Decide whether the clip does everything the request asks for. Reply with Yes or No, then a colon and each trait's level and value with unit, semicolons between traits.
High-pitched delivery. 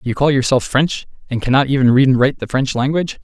No: low, 130 Hz